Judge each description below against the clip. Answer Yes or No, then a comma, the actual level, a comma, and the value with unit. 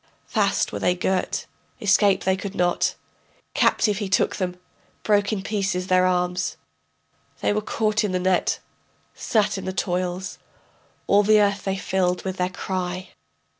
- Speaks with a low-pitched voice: No, high, 190 Hz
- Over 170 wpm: No, average, 155 wpm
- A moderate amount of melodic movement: No, narrow, 1.9 semitones